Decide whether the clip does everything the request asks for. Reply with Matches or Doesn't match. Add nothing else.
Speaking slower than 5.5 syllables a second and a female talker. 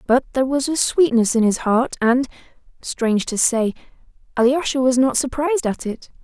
Matches